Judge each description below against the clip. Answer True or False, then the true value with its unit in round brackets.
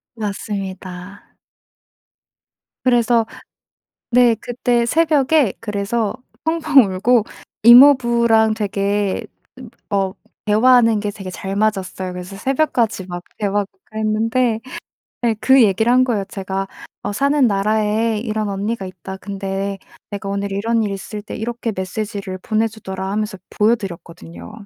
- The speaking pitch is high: True (215 Hz)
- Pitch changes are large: False (3.1 semitones)